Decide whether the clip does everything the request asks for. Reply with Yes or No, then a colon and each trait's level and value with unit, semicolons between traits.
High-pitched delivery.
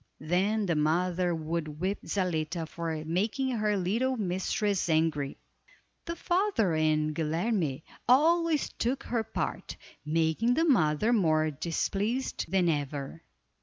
No: medium, 180 Hz